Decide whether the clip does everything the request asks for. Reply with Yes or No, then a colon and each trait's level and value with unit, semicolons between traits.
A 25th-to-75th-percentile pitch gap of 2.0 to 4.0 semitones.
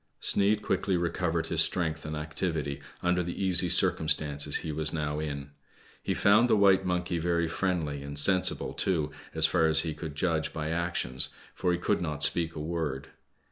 Yes: average, 2.8 semitones